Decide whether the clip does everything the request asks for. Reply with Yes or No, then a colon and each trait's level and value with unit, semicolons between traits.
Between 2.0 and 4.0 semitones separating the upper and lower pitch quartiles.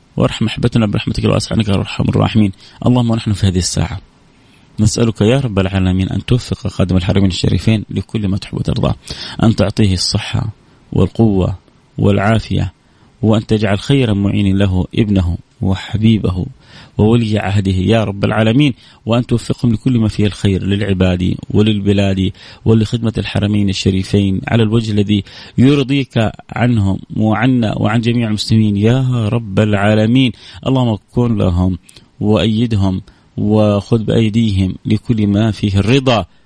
Yes: average, 2.8 semitones